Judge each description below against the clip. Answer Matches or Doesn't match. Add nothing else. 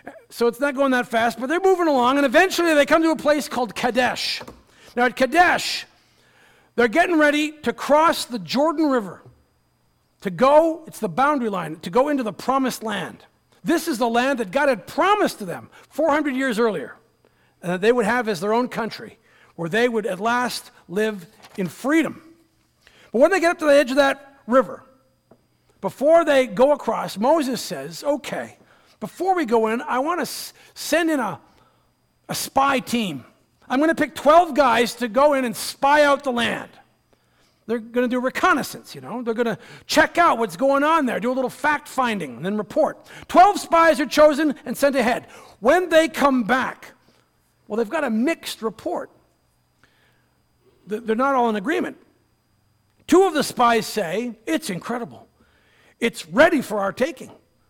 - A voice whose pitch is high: Matches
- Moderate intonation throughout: Matches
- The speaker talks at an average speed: Matches